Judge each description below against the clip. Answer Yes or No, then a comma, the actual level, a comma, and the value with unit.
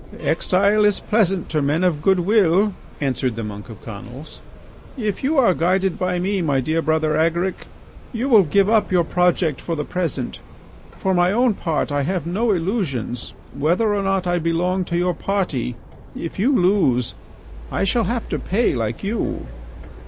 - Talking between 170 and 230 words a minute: Yes, average, 175 wpm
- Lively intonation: No, average, 4.4 semitones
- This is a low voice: No, medium, 180 Hz